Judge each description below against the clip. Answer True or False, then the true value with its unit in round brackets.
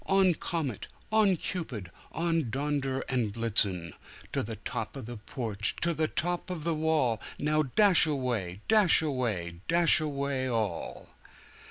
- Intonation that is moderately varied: False (6.6 semitones)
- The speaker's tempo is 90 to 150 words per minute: True (145 wpm)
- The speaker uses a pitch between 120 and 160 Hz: True (140 Hz)